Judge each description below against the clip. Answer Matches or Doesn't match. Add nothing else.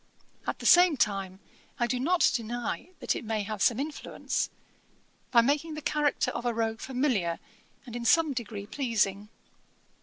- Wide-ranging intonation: Doesn't match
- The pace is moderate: Matches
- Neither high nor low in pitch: Doesn't match